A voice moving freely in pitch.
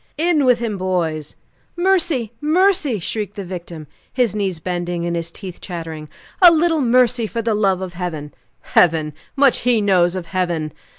Yes: wide, 6.4 semitones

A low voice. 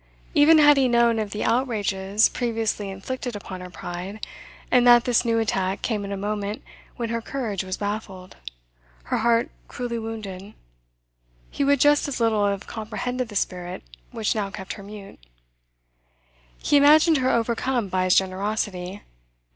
No: high, 220 Hz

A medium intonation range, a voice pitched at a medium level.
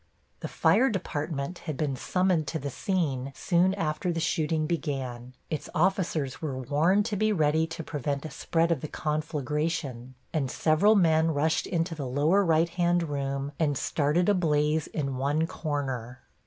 Yes: average, 3.2 semitones; medium, 155 Hz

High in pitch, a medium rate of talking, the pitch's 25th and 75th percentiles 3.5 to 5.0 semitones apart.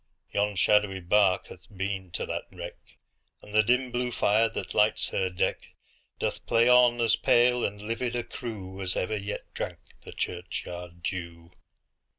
No: low, 105 Hz; average, 150 wpm; average, 4.0 semitones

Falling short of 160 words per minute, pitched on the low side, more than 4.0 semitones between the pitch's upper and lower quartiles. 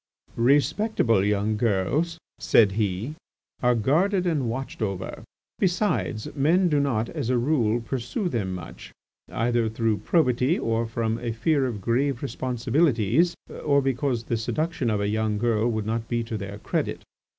Yes: average, 150 wpm; low, 120 Hz; average, 4.5 semitones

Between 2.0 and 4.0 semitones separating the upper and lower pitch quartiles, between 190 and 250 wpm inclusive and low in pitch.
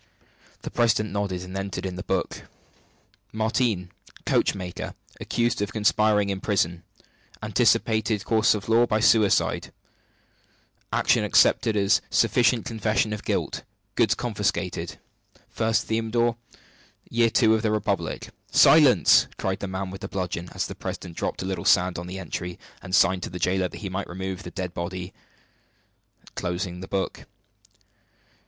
No: average, 3.2 semitones; average, 145 wpm; low, 100 Hz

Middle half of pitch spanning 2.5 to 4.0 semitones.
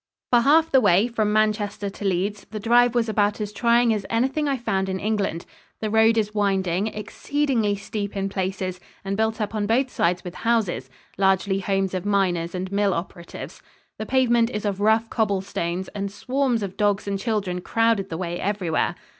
Yes: average, 2.9 semitones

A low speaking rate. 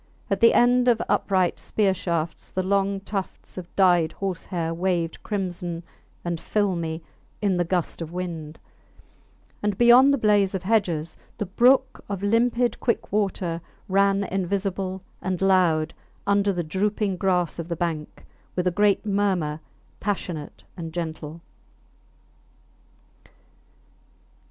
Yes: slow, 130 wpm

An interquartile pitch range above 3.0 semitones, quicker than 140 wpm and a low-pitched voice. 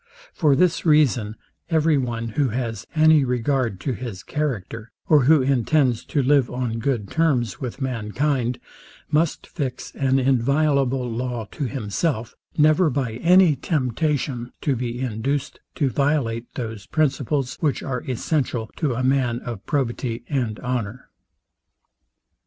No: average, 3.7 semitones; slow, 135 wpm; low, 130 Hz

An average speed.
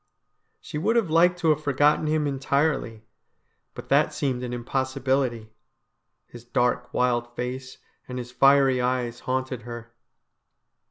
No: slow, 130 wpm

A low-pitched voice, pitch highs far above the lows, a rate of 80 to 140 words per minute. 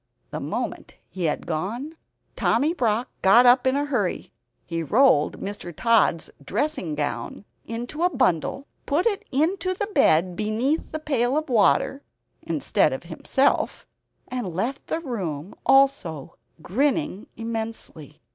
No: high, 235 Hz; wide, 7.6 semitones; slow, 135 wpm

